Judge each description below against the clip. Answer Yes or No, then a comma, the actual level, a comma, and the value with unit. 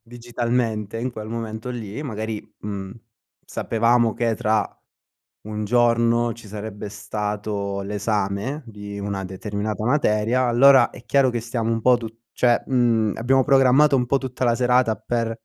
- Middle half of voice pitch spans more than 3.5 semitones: No, narrow, 2.6 semitones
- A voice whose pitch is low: Yes, low, 115 Hz